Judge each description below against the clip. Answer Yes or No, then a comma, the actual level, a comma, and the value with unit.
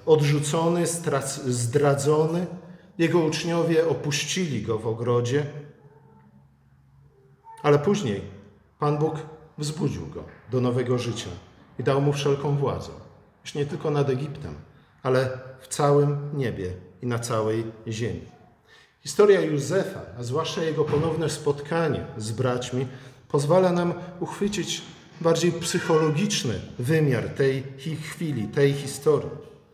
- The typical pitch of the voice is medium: Yes, medium, 145 Hz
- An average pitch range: Yes, average, 4.2 semitones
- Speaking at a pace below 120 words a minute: Yes, slow, 110 wpm